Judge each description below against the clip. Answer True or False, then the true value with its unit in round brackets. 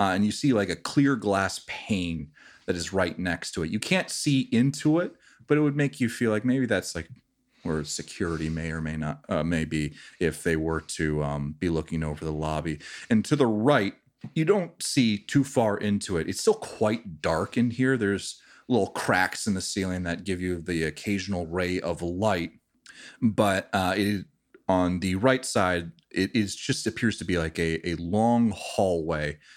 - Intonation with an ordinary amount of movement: False (6.2 semitones)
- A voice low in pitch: True (95 Hz)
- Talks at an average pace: True (195 wpm)